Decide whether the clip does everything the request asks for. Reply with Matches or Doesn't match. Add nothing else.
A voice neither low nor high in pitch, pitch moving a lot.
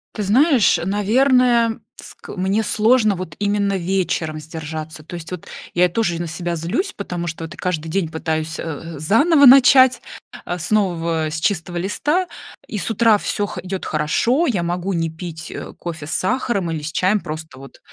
Doesn't match